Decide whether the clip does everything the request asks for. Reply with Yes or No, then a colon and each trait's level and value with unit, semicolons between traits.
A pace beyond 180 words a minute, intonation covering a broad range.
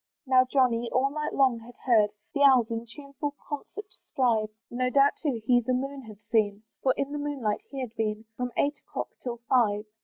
No: average, 195 wpm; average, 3.4 semitones